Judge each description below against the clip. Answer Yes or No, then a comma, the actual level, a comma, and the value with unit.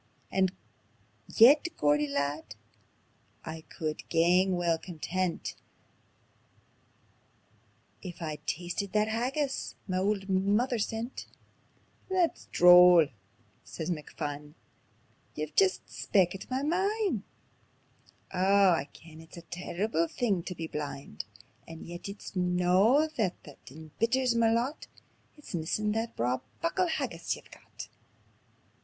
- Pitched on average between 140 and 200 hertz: Yes, medium, 185 Hz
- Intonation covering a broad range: Yes, wide, 5.7 semitones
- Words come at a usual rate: No, slow, 110 wpm